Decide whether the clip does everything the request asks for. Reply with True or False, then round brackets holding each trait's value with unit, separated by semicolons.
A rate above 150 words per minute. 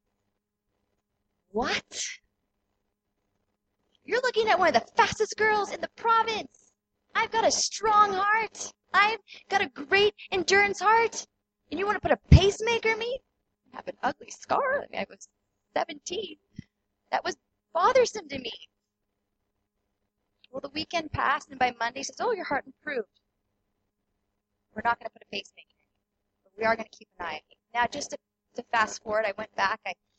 True (175 wpm)